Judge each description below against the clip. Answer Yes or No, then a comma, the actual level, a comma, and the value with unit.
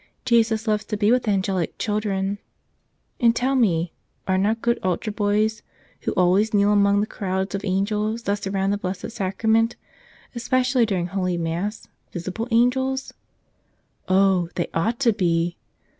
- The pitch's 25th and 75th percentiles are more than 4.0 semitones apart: No, average, 3.2 semitones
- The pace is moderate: Yes, average, 150 wpm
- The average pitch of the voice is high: Yes, high, 205 Hz